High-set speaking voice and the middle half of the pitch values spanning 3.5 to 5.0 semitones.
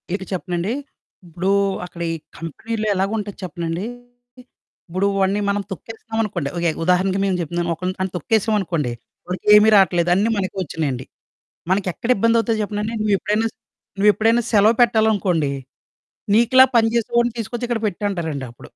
Yes: high, 195 Hz; average, 4.0 semitones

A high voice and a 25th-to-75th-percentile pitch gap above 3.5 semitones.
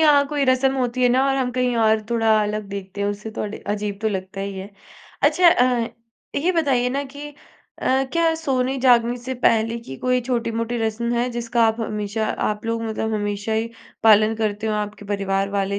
No: high, 230 Hz; average, 3.2 semitones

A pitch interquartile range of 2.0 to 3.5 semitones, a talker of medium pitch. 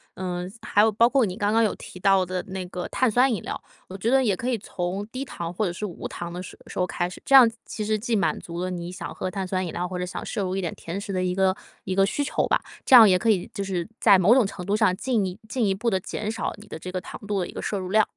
No: average, 3.1 semitones; high, 195 Hz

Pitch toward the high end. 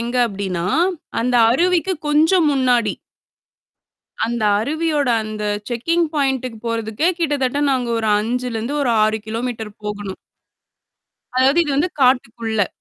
Yes: high, 245 Hz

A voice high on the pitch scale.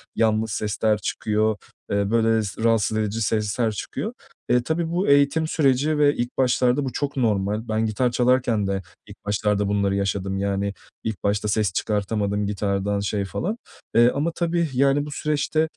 No: low, 110 Hz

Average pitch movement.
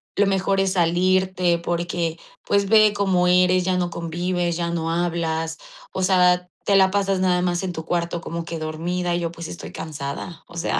No: narrow, 1.7 semitones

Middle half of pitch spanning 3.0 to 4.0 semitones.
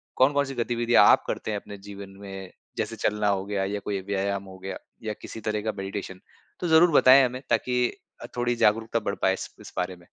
Yes: average, 3.7 semitones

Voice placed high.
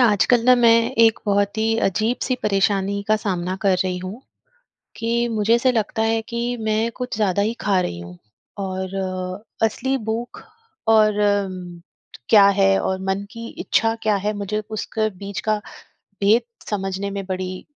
Yes: high, 210 Hz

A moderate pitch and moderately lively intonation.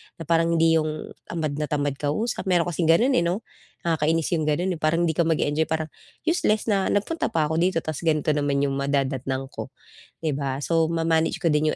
No: medium, 160 Hz; narrow, 2.3 semitones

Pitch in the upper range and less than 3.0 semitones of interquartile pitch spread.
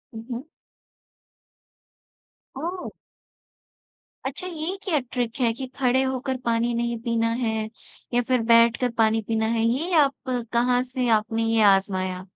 Yes: high, 240 Hz; narrow, 2.5 semitones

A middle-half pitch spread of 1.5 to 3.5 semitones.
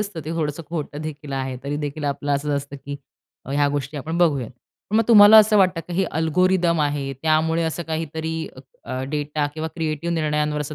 Yes: narrow, 2.5 semitones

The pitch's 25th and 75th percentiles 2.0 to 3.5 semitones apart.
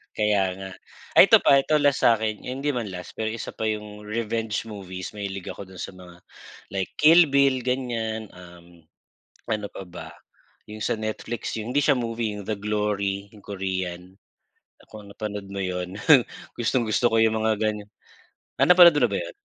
Yes: average, 2.9 semitones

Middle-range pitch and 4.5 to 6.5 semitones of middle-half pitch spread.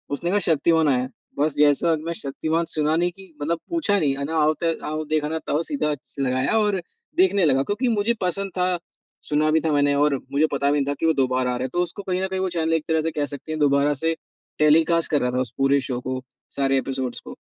No: medium, 155 Hz; average, 3.3 semitones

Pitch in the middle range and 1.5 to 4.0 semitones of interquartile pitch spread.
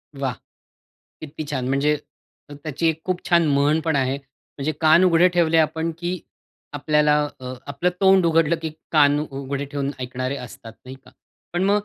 Yes: medium, 150 Hz; average, 3.1 semitones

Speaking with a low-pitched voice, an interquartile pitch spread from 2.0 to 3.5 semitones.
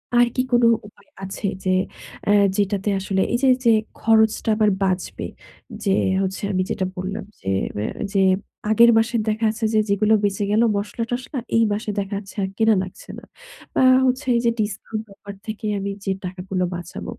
No: high, 210 Hz; narrow, 2.6 semitones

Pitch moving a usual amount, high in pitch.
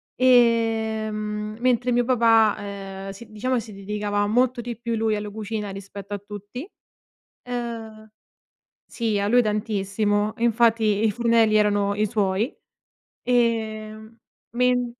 No: narrow, 2.2 semitones; high, 220 Hz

